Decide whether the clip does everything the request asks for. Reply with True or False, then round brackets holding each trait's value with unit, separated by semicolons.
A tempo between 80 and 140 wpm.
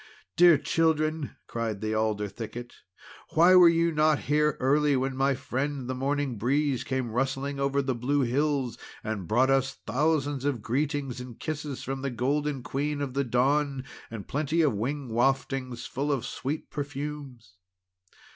False (155 wpm)